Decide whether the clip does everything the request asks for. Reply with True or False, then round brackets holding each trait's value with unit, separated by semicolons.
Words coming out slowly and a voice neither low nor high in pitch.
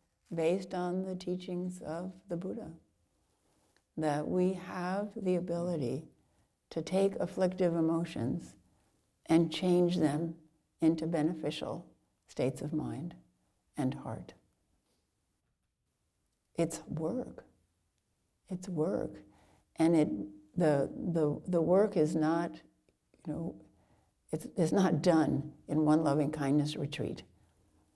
True (105 wpm; 160 Hz)